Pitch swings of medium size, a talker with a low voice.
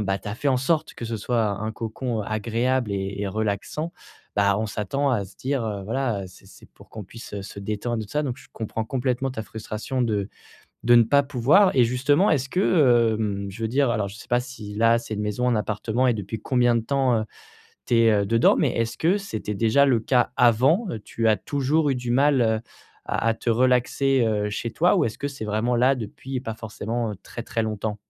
Yes: average, 3.4 semitones; low, 115 Hz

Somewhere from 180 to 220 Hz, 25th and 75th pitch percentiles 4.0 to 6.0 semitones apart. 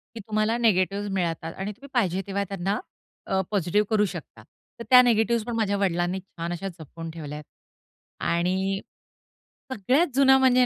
Yes: high, 195 Hz; average, 4.4 semitones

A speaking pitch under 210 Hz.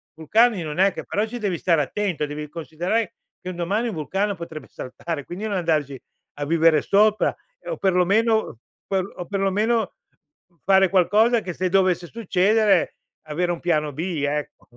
Yes: medium, 185 Hz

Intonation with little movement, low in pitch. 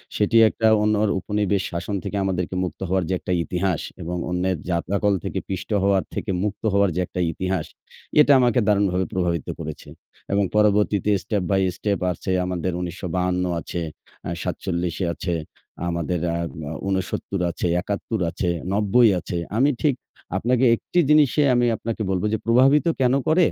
No: average, 3.0 semitones; very low, 95 Hz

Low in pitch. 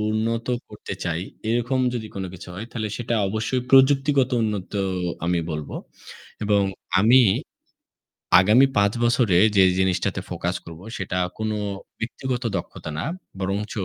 Yes: low, 110 Hz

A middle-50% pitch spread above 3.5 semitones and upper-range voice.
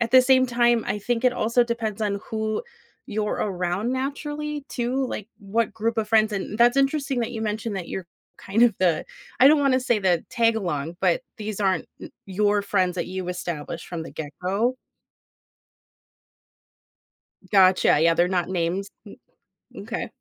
Yes: average, 4.5 semitones; high, 215 Hz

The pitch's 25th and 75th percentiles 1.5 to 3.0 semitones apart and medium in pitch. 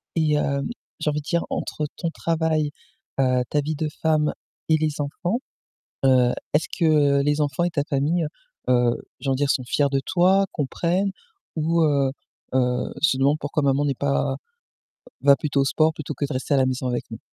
Yes: narrow, 2.6 semitones; medium, 145 Hz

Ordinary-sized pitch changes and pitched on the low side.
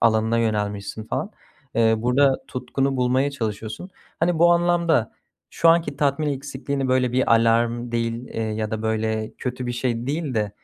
Yes: average, 3.8 semitones; low, 120 Hz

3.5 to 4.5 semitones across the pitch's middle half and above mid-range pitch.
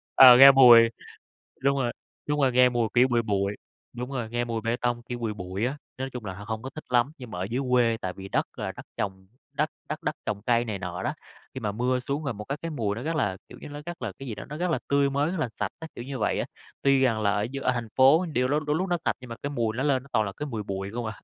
No: average, 4.0 semitones; low, 125 Hz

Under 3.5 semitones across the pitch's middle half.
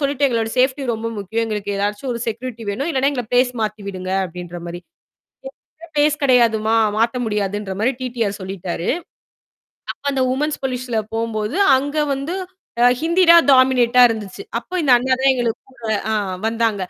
No: average, 3.9 semitones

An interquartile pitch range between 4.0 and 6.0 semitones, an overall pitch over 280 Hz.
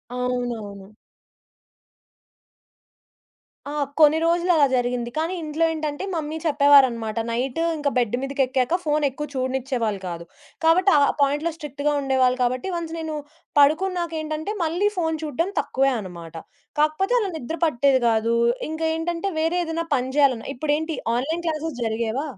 Yes: average, 4.5 semitones; very high, 290 Hz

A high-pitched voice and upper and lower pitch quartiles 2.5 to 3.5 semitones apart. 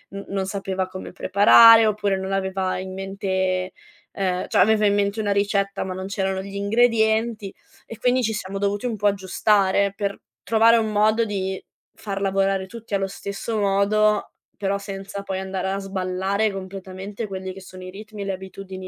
No: high, 195 Hz; narrow, 1.6 semitones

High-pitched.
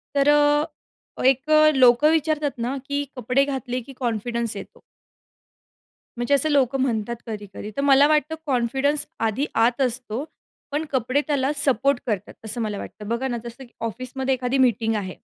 Yes: very high, 260 Hz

